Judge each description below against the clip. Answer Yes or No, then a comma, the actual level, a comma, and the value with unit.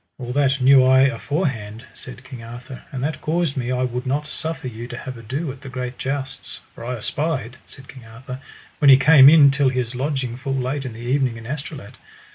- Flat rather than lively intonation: Yes, narrow, 2.1 semitones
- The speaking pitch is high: No, low, 130 Hz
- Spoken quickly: Yes, fast, 215 wpm